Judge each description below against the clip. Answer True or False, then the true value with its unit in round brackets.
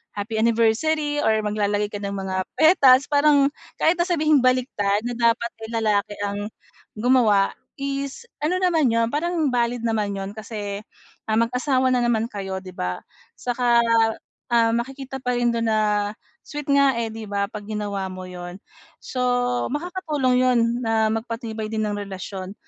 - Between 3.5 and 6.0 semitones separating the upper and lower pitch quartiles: True (4.3 semitones)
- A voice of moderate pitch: False (230 Hz)